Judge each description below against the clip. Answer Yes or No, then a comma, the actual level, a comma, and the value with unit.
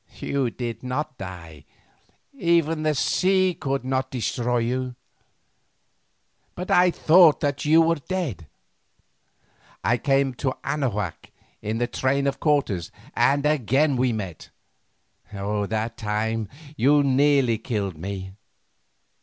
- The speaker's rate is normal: No, slow, 115 wpm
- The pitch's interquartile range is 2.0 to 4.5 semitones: No, average, 5.2 semitones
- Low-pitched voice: Yes, low, 130 Hz